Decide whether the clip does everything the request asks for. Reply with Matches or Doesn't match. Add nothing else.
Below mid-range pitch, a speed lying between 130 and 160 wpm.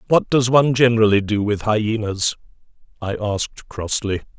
Matches